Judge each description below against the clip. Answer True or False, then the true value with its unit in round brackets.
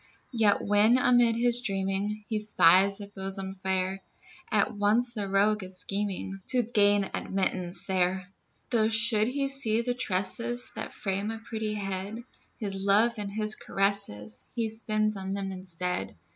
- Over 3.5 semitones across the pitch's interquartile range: False (2.6 semitones)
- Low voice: False (205 Hz)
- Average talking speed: True (150 wpm)